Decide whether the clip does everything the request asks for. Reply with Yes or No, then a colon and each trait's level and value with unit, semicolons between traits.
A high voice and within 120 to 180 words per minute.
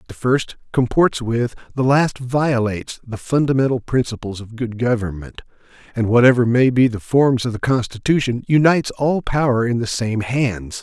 No: low, 120 Hz; average, 160 wpm